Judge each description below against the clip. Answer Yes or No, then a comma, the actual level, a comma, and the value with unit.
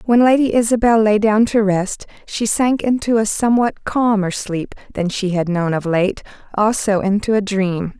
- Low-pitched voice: No, high, 210 Hz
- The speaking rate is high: No, average, 180 wpm